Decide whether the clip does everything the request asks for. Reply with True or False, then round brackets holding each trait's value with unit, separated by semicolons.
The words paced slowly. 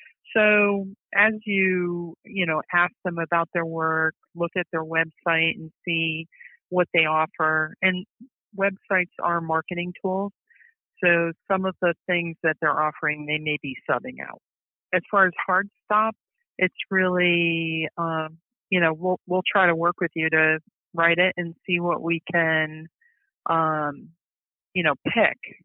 False (155 wpm)